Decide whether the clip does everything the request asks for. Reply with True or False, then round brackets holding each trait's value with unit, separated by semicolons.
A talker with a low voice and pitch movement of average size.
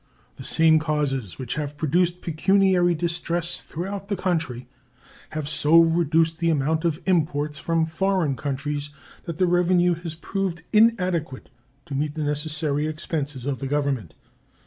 False (160 Hz; 3.0 semitones)